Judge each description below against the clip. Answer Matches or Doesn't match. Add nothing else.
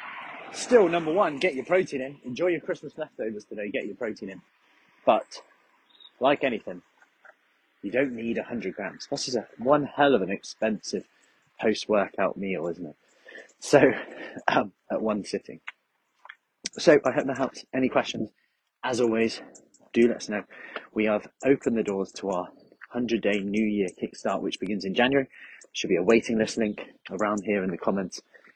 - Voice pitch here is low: Matches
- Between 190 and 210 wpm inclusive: Doesn't match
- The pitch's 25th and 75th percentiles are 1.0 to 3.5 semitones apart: Doesn't match